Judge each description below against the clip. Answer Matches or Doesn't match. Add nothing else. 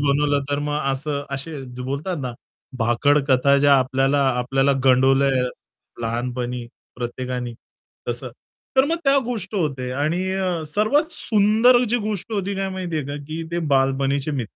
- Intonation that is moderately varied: Doesn't match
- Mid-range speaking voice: Matches